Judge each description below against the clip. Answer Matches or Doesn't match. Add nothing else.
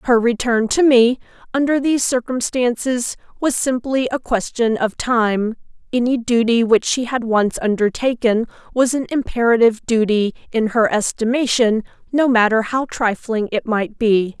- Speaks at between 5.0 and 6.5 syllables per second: Doesn't match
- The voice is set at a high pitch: Matches